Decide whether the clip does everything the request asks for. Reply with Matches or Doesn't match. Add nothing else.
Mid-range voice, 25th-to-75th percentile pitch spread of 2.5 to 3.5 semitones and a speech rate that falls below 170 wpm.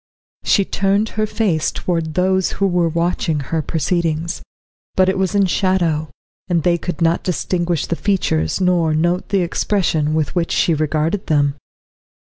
Matches